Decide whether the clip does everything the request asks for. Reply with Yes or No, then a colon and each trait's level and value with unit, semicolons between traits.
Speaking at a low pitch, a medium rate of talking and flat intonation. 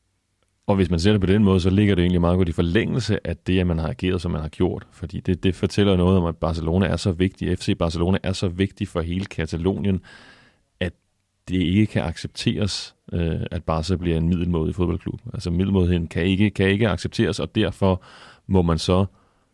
Yes: very low, 95 Hz; average, 210 wpm; narrow, 2.3 semitones